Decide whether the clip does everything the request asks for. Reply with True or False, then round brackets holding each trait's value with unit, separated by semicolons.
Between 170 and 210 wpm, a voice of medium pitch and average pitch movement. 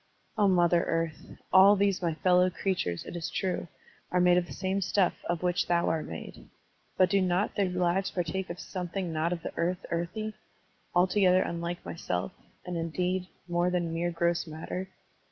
False (180 wpm; 180 Hz; 1.7 semitones)